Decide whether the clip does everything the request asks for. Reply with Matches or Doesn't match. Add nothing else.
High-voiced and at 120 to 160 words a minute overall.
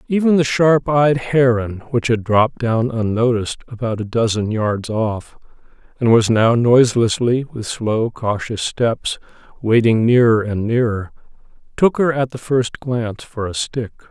Doesn't match